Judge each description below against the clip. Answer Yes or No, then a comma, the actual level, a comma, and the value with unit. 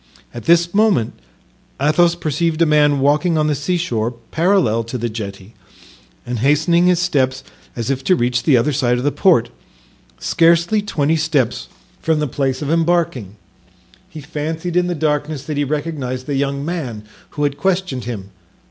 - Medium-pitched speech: Yes, medium, 150 Hz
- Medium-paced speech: Yes, average, 165 wpm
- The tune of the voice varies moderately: Yes, average, 4.7 semitones